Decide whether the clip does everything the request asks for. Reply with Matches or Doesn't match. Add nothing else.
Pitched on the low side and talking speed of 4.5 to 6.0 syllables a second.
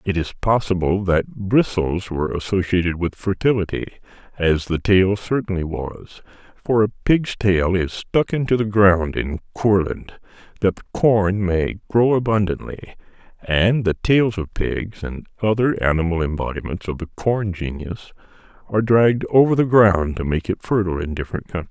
Matches